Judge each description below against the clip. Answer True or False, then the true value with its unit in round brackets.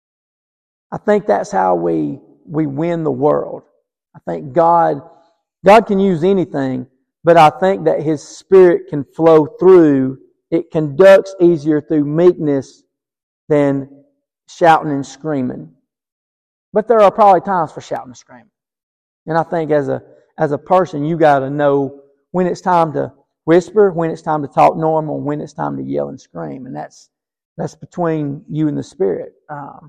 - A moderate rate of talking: True (165 wpm)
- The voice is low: False (155 Hz)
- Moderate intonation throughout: True (3.9 semitones)